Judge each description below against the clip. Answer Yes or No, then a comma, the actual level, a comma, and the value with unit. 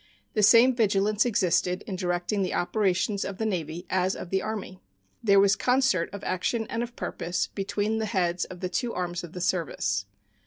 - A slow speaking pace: No, average, 190 wpm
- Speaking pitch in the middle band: No, high, 195 Hz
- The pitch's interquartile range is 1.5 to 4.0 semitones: Yes, average, 3.2 semitones